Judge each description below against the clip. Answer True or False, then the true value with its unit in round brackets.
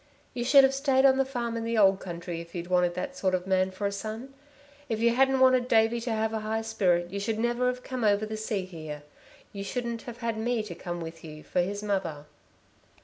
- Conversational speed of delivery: False (240 wpm)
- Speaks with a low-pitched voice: False (220 Hz)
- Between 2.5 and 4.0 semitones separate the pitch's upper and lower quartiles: False (4.5 semitones)